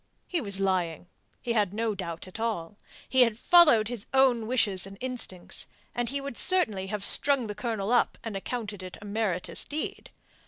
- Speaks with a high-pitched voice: Yes, high, 220 Hz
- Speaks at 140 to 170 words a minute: No, average, 180 wpm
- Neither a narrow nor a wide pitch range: Yes, average, 4.1 semitones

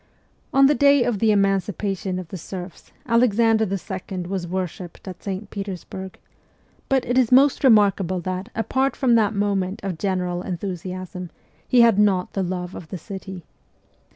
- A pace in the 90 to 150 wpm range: No, average, 160 wpm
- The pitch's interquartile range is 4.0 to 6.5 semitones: No, average, 3.5 semitones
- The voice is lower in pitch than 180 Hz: No, high, 195 Hz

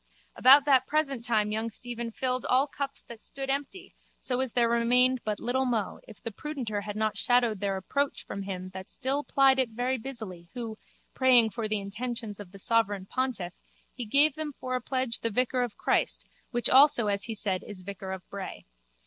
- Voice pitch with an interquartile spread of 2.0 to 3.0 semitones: No, average, 3.9 semitones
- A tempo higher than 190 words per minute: Yes, average, 200 wpm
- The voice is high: Yes, high, 235 Hz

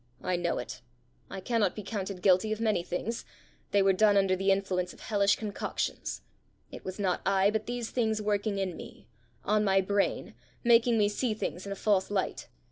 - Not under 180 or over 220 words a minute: Yes, average, 195 wpm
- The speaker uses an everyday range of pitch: No, narrow, 2.3 semitones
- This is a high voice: Yes, high, 200 Hz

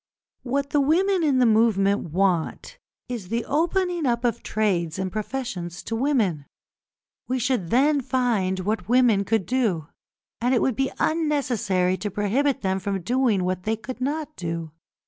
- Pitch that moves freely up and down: Yes, wide, 6.0 semitones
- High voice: Yes, high, 230 Hz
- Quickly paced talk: No, average, 160 wpm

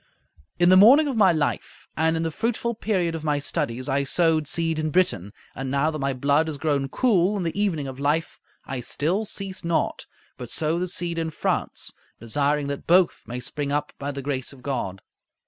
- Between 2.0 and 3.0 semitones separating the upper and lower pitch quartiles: No, average, 4.0 semitones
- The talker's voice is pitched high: No, medium, 155 Hz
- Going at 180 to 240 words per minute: Yes, fast, 205 wpm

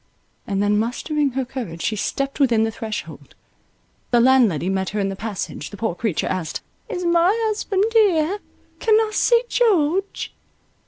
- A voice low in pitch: No, very high, 255 Hz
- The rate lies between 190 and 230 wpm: No, average, 160 wpm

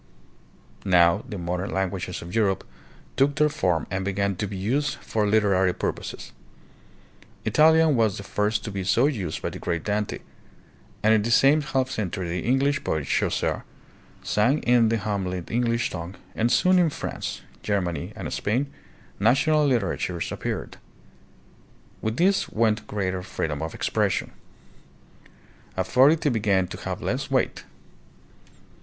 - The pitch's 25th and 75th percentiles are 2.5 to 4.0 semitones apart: No, wide, 5.5 semitones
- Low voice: Yes, low, 105 Hz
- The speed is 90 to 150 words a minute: Yes, average, 145 wpm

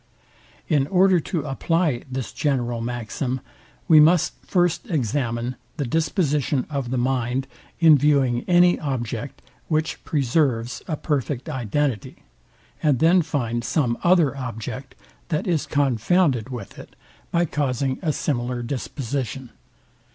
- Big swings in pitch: No, average, 4.2 semitones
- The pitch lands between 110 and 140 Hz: Yes, low, 135 Hz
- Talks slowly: Yes, slow, 120 wpm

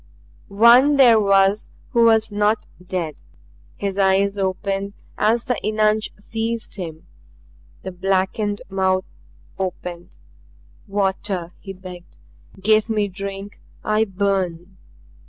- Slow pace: Yes, slow, 105 wpm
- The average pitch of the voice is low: No, high, 200 Hz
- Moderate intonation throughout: No, narrow, 2.2 semitones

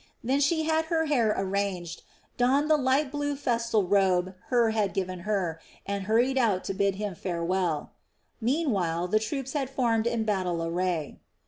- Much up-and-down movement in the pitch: Yes, wide, 6.2 semitones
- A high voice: Yes, high, 215 Hz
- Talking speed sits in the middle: Yes, average, 160 wpm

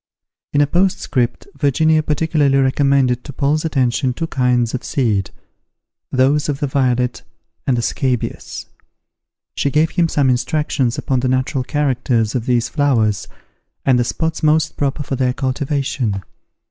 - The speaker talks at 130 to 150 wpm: Yes, average, 145 wpm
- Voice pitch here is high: No, low, 135 Hz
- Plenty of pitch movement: No, average, 2.9 semitones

